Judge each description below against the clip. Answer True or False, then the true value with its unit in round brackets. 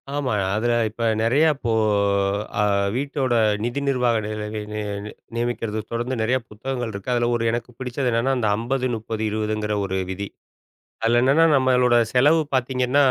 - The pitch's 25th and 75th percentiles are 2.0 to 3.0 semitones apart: True (2.7 semitones)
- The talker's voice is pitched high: False (120 Hz)